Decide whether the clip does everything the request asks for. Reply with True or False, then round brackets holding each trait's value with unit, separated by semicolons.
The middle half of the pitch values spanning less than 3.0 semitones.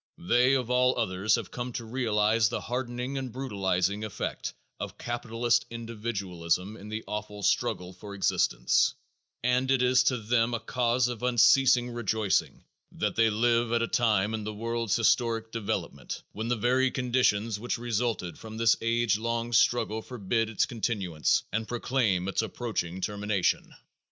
True (2.5 semitones)